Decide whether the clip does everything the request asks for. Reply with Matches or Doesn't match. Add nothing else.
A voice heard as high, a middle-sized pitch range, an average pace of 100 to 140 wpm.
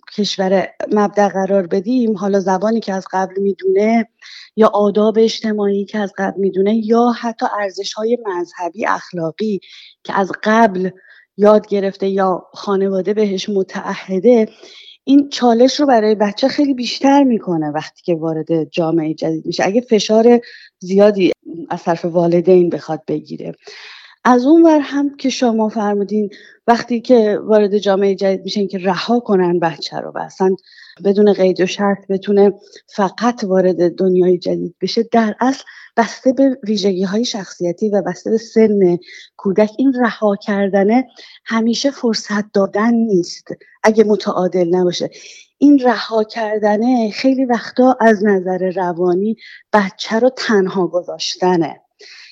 Matches